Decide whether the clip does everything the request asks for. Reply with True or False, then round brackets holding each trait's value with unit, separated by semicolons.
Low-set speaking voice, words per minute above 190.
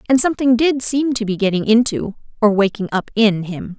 False (225 Hz; 205 wpm)